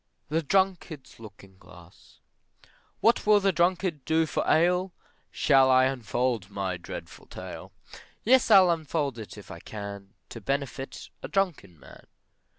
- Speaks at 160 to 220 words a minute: No, average, 140 wpm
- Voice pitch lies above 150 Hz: No, low, 135 Hz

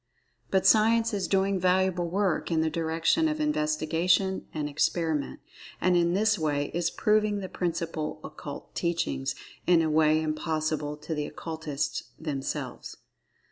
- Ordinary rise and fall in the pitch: Yes, average, 3.6 semitones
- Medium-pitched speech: Yes, medium, 165 Hz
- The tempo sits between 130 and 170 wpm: Yes, average, 140 wpm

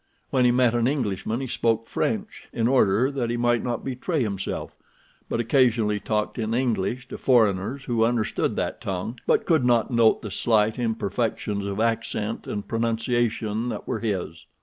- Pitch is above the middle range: No, low, 115 Hz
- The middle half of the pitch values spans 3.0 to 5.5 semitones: No, narrow, 2.5 semitones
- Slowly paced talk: No, average, 170 wpm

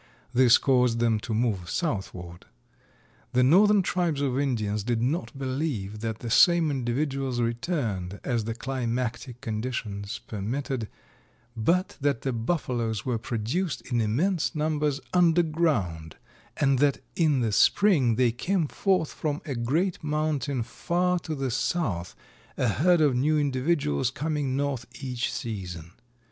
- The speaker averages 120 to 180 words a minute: Yes, slow, 135 wpm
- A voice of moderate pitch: No, low, 130 Hz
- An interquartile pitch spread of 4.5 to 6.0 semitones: Yes, average, 5.1 semitones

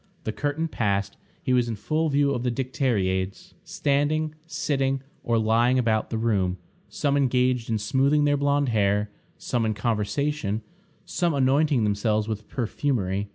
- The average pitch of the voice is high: No, low, 125 Hz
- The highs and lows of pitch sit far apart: No, average, 4.9 semitones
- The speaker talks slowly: No, average, 150 wpm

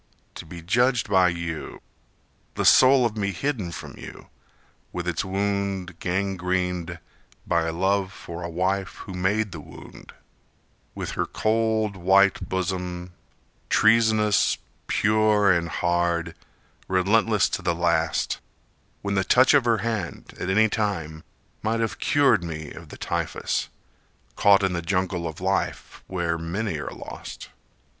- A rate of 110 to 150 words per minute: Yes, slow, 135 wpm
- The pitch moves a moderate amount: Yes, average, 3.6 semitones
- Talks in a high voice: No, very low, 95 Hz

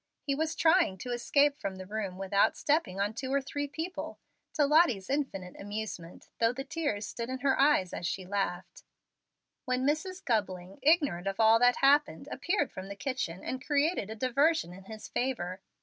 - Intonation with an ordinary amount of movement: No, wide, 6.8 semitones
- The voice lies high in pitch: Yes, high, 245 Hz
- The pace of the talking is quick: No, average, 185 wpm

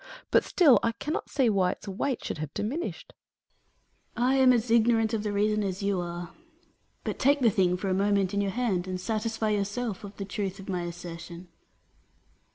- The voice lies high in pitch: Yes, high, 205 Hz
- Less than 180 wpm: No, average, 195 wpm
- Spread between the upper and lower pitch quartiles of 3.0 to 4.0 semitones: Yes, average, 3.7 semitones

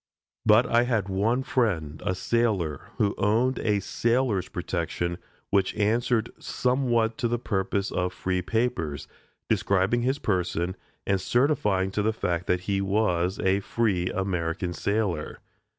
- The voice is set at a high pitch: No, low, 100 Hz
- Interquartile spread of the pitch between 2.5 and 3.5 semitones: No, average, 4.2 semitones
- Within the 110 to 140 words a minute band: Yes, slow, 135 wpm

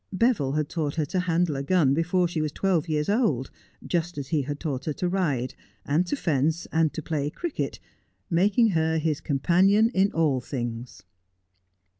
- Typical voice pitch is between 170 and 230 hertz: No, medium, 160 Hz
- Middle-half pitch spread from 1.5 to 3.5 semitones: No, average, 4.1 semitones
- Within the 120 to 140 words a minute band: No, average, 180 wpm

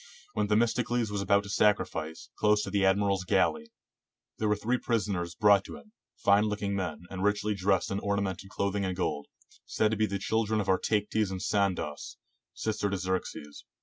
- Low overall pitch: Yes, low, 100 Hz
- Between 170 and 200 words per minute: Yes, average, 180 wpm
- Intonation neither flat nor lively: No, narrow, 1.8 semitones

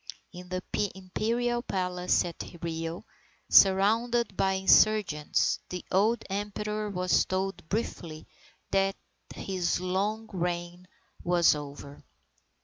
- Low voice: No, high, 190 Hz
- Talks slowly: Yes, slow, 100 wpm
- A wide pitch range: No, average, 3.1 semitones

